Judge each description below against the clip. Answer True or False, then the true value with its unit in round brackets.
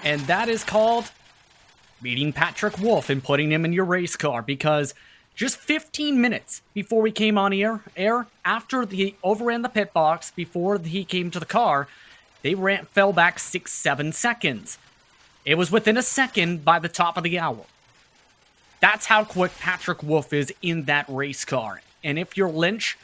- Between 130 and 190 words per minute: True (175 wpm)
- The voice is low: False (180 Hz)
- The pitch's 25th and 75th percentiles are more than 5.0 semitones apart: True (5.4 semitones)